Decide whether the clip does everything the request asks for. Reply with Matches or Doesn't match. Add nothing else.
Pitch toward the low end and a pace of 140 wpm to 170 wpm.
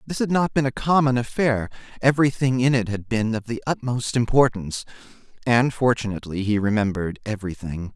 Matches